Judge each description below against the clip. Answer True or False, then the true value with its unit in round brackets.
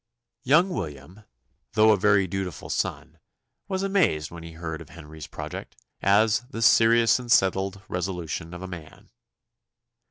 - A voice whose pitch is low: True (95 Hz)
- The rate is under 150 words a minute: True (140 wpm)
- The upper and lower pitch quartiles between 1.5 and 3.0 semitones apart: False (5.4 semitones)